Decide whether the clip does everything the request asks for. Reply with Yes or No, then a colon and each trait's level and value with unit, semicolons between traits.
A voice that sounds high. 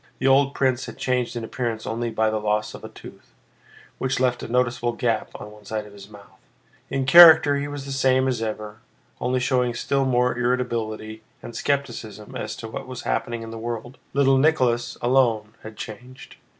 No: low, 120 Hz